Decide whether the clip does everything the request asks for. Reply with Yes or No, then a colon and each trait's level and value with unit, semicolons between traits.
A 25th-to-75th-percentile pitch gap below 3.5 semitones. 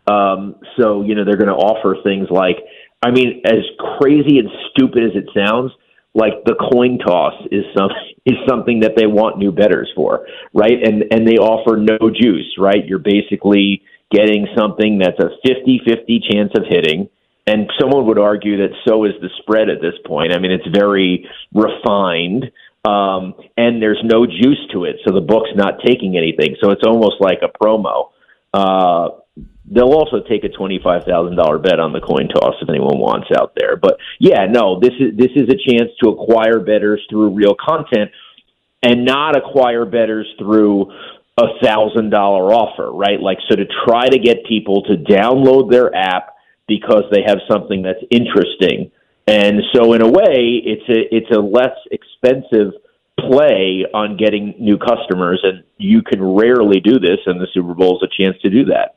Yes: average, 3.0 semitones